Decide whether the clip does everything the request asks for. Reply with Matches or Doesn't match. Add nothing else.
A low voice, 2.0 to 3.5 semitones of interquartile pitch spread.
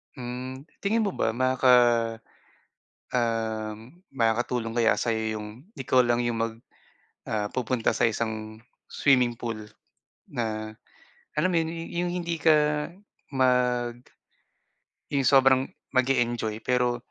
Matches